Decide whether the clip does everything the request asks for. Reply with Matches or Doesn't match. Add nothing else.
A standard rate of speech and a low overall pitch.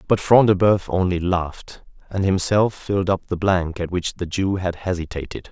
Matches